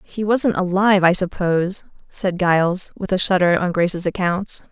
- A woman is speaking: Yes, female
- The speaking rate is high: No, average, 165 wpm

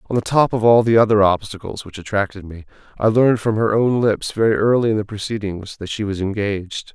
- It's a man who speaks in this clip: Yes, male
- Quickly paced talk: Yes, fast, 225 wpm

